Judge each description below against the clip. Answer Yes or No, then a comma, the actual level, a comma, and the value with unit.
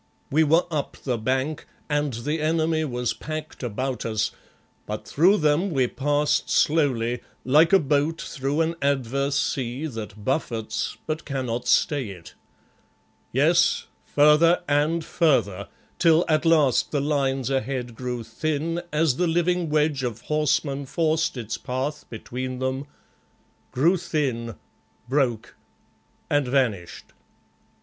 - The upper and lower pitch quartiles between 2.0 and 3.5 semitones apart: No, average, 4.0 semitones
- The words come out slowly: Yes, slow, 125 wpm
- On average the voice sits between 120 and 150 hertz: Yes, medium, 140 Hz